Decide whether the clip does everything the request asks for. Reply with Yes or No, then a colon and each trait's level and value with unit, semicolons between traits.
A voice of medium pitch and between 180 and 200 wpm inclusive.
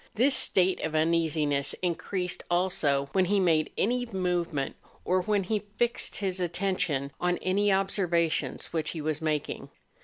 No: medium, 180 Hz; average, 145 wpm